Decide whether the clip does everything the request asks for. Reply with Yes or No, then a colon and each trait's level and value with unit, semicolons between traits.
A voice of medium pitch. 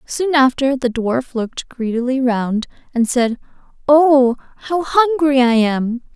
No: very high, 260 Hz